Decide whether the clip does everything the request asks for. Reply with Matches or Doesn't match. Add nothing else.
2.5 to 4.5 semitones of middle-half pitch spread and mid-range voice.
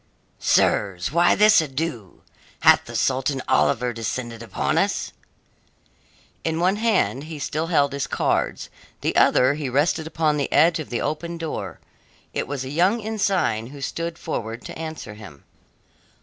Doesn't match